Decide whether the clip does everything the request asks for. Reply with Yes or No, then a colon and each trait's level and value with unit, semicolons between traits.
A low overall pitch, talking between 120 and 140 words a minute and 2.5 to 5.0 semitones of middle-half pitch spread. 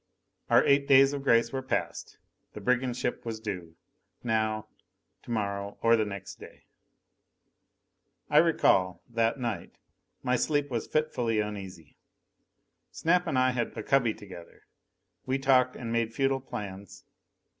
Yes: low, 115 Hz; slow, 135 wpm; average, 4.1 semitones